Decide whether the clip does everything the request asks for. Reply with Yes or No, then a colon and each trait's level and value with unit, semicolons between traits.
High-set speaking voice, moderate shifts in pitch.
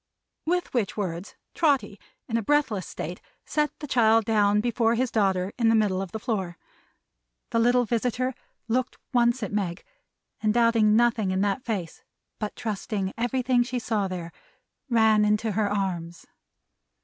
Yes: high, 220 Hz; average, 3.3 semitones